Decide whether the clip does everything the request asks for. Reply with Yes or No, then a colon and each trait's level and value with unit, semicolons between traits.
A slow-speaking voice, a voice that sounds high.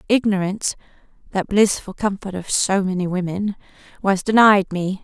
Yes: slow, 105 wpm; high, 195 Hz